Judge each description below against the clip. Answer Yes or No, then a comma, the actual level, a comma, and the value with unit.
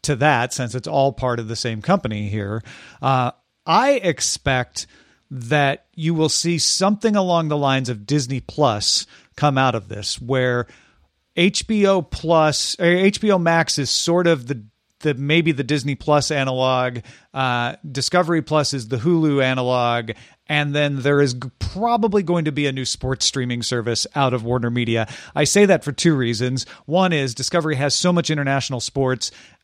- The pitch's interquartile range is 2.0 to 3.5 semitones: No, average, 4.1 semitones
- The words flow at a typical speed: Yes, average, 170 wpm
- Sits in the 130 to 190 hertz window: Yes, medium, 140 Hz